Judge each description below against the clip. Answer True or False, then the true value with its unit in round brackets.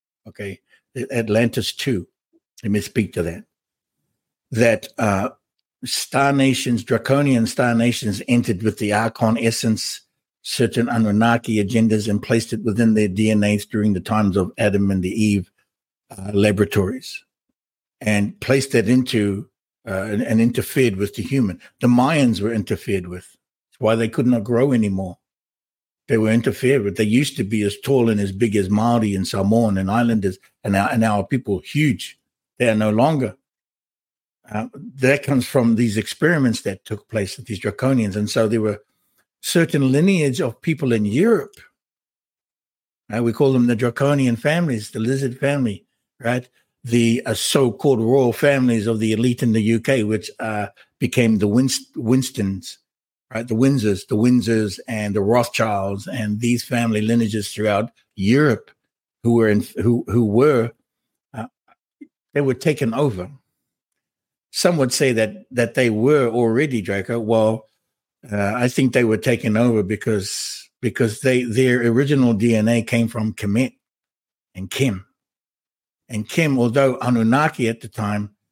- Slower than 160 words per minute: True (150 wpm)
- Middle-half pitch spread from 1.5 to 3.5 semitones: True (3.2 semitones)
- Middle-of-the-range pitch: False (115 Hz)